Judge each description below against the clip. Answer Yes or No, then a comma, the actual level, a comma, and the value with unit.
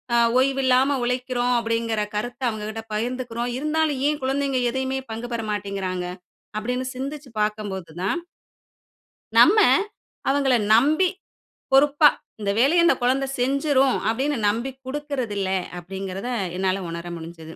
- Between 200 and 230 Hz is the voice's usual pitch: No, high, 245 Hz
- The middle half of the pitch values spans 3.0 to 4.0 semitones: No, average, 4.4 semitones